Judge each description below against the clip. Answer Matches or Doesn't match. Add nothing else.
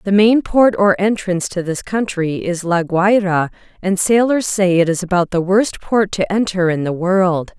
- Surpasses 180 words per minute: Matches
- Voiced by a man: Doesn't match